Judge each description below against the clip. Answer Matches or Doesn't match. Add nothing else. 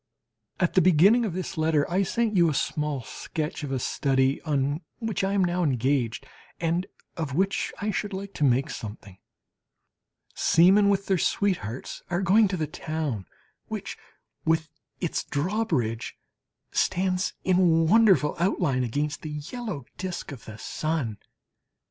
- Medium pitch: Matches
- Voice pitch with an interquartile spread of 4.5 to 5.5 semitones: Matches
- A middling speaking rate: Matches